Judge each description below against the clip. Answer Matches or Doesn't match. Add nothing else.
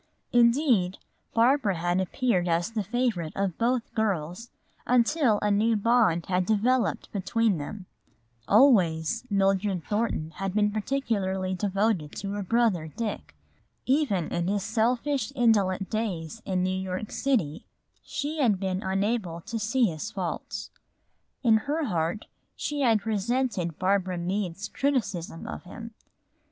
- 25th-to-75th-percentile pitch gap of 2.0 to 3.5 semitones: Doesn't match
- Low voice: Doesn't match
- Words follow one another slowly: Matches